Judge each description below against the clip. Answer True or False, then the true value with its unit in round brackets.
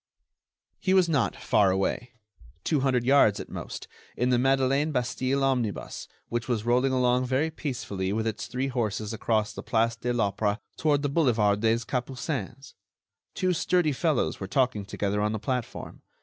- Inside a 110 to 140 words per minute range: False (155 wpm)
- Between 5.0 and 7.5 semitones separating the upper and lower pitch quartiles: False (4.0 semitones)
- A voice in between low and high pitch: False (125 Hz)